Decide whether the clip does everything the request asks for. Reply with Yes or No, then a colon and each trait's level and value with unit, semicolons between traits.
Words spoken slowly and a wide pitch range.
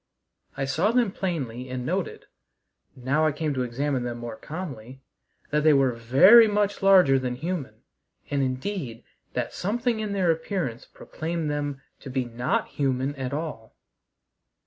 No: average, 150 wpm; wide, 5.7 semitones